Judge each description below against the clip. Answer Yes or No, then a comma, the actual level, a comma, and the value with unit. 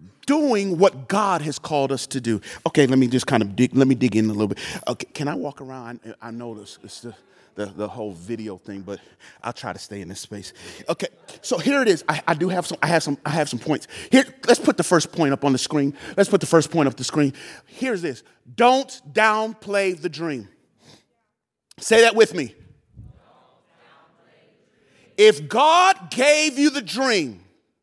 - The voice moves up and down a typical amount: No, wide, 8.8 semitones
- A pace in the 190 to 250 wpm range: Yes, fast, 205 wpm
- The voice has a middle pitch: Yes, medium, 150 Hz